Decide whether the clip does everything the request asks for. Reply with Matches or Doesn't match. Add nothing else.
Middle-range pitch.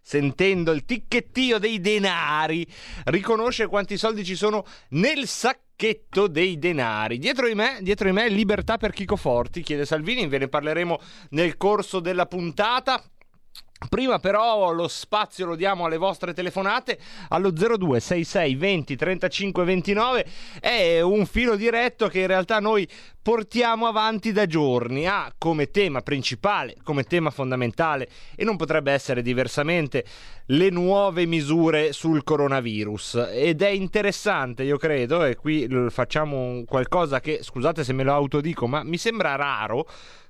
Matches